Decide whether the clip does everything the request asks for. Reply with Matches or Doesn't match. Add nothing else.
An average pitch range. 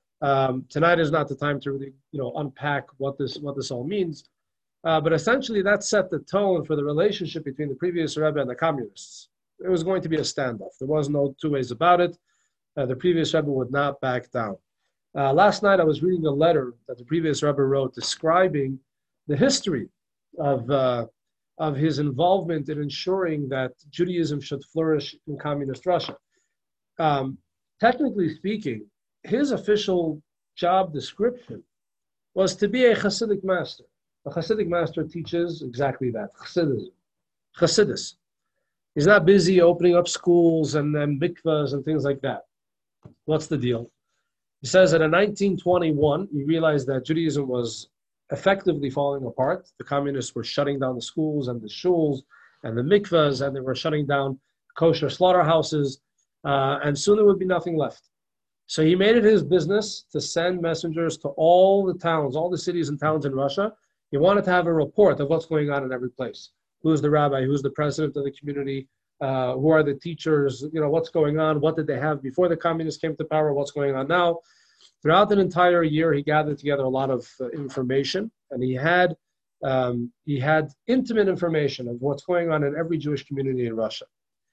Matches